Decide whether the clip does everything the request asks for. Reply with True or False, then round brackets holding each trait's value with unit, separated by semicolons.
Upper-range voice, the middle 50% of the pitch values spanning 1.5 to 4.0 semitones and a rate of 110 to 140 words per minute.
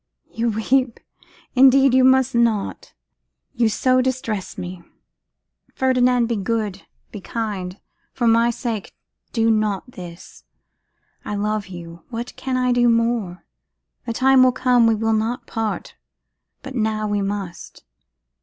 True (230 Hz; 3.3 semitones; 135 wpm)